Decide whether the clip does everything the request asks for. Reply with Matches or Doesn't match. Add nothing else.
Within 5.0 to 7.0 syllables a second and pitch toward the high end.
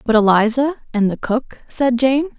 Doesn't match